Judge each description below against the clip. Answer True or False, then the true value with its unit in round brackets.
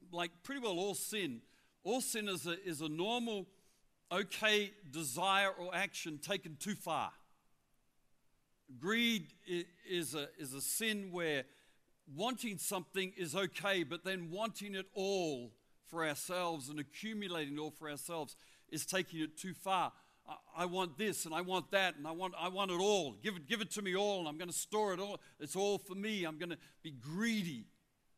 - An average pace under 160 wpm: False (185 wpm)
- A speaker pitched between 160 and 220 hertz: True (185 Hz)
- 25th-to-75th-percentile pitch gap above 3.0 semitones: True (3.6 semitones)